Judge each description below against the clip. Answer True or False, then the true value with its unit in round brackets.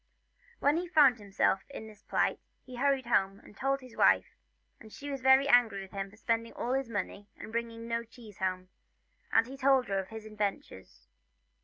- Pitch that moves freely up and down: False (4.8 semitones)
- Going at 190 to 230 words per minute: True (195 wpm)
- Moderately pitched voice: False (230 Hz)